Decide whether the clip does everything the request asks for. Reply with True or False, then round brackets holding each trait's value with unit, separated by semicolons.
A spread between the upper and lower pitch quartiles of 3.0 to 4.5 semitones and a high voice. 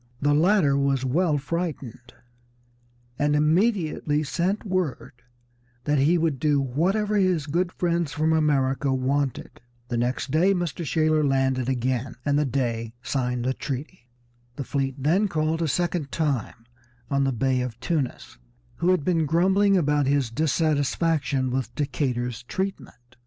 False (4.2 semitones; 145 Hz)